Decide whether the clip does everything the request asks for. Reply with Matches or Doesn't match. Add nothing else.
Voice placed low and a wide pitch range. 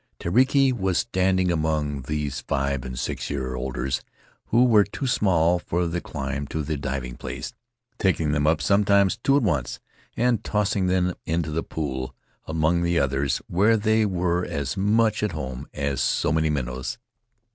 Matches